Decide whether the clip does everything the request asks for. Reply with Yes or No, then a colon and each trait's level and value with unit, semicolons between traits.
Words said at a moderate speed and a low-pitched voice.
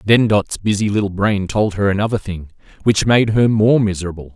Yes: average, 195 wpm; low, 100 Hz